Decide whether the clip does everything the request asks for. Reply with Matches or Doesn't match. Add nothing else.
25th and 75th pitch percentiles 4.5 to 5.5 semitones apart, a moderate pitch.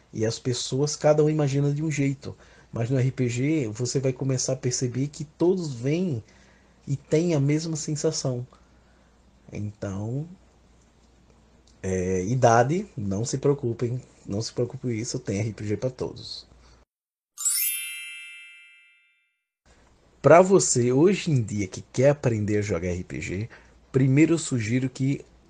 Doesn't match